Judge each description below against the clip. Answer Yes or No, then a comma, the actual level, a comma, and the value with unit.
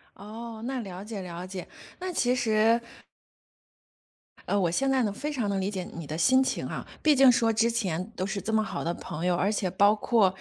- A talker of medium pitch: No, high, 210 Hz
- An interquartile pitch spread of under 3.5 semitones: No, average, 4.1 semitones